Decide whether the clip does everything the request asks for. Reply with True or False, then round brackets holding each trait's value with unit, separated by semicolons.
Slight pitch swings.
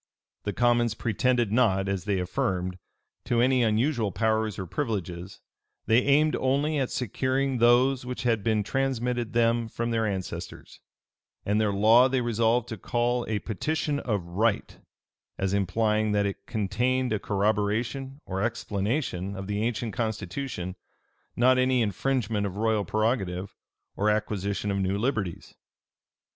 False (3.6 semitones)